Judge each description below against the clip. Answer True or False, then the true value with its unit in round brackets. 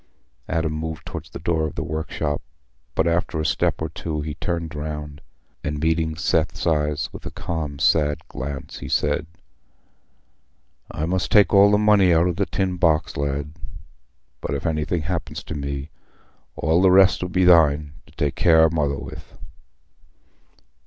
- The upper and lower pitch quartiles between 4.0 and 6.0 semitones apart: False (2.4 semitones)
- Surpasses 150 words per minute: True (165 wpm)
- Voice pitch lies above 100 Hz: False (80 Hz)